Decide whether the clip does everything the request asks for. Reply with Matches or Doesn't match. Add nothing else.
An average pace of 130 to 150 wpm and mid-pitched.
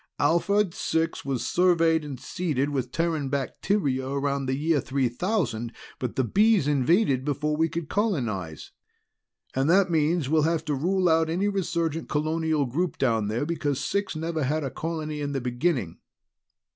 Doesn't match